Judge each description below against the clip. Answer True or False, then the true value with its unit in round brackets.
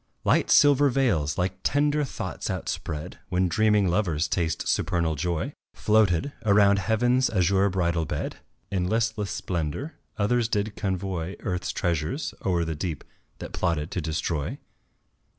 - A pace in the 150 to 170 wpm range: False (135 wpm)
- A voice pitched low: True (95 Hz)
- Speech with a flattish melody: False (4.6 semitones)